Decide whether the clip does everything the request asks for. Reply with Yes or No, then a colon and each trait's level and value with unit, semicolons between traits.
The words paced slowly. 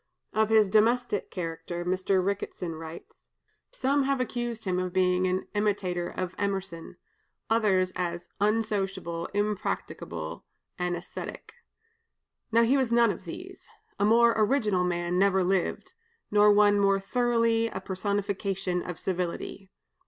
Yes: slow, 130 wpm